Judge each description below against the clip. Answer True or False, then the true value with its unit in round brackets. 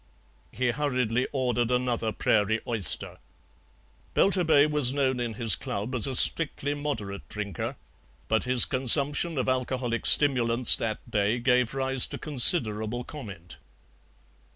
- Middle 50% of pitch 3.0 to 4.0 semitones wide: True (3.4 semitones)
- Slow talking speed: True (120 wpm)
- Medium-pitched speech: False (125 Hz)